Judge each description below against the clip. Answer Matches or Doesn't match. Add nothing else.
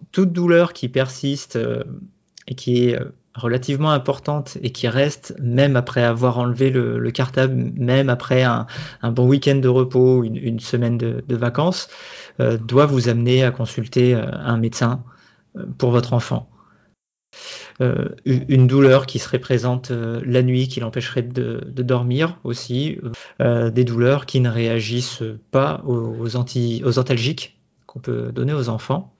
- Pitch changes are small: Matches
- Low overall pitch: Matches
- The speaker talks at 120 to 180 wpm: Matches